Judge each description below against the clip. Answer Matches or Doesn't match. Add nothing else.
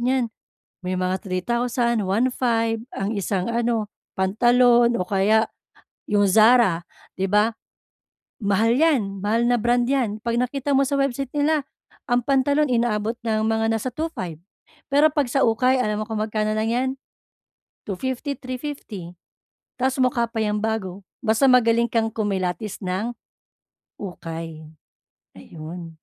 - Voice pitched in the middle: Doesn't match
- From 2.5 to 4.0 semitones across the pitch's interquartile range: Matches